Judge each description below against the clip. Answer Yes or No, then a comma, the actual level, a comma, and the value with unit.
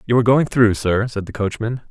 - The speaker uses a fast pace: Yes, fast, 250 wpm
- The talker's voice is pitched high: No, low, 115 Hz